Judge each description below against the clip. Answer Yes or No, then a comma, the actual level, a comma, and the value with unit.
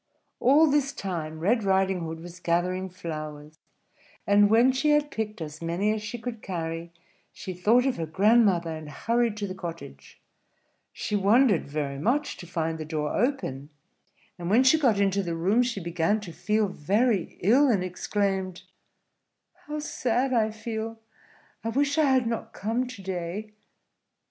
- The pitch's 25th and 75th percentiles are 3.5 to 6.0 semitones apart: Yes, wide, 5.6 semitones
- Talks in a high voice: Yes, high, 200 Hz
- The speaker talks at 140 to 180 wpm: Yes, average, 165 wpm